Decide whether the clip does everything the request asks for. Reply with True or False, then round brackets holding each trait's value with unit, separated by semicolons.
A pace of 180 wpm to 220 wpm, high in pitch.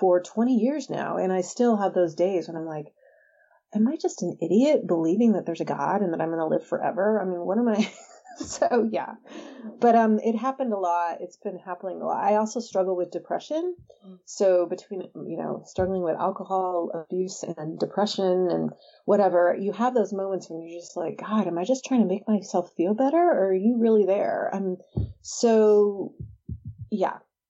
True (200 wpm; 195 Hz)